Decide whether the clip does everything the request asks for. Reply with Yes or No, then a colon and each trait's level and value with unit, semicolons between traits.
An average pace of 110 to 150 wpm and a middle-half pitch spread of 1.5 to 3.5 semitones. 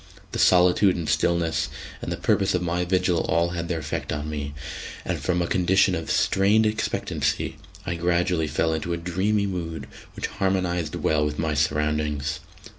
No: average, 170 wpm; average, 2.7 semitones